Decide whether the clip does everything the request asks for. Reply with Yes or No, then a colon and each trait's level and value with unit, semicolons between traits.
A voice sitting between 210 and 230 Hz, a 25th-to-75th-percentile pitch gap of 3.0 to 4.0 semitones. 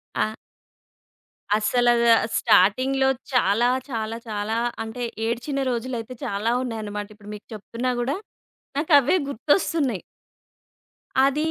No: high, 240 Hz; average, 3.6 semitones